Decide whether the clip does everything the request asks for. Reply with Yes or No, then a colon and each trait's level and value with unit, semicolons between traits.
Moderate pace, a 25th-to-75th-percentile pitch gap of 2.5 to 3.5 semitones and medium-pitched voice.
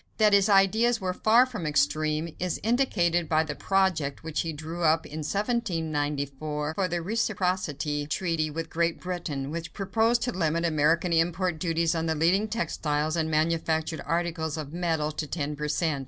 Yes: average, 170 wpm; average, 3.1 semitones; medium, 165 Hz